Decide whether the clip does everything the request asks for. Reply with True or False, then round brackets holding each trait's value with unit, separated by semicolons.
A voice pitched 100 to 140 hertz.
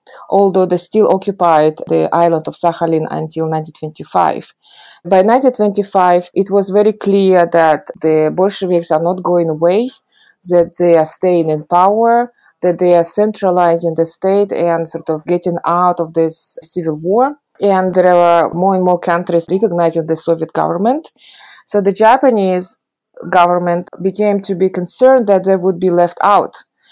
False (180 Hz)